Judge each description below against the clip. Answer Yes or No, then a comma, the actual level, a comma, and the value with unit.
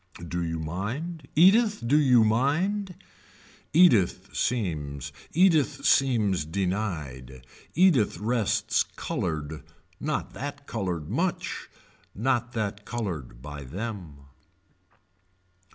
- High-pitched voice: No, low, 110 Hz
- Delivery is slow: Yes, slow, 90 wpm